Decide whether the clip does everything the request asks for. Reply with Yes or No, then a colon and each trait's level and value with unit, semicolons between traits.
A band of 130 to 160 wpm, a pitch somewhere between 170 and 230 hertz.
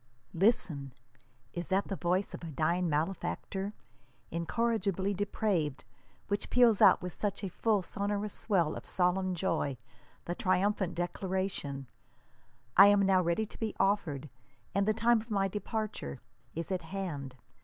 Yes: average, 145 wpm; high, 190 Hz